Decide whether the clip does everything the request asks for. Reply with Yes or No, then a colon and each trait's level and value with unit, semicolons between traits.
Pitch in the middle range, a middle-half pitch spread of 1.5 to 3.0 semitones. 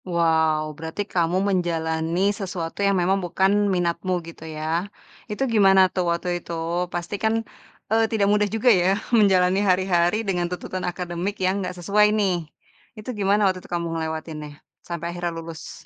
Yes: medium, 180 Hz; average, 2.7 semitones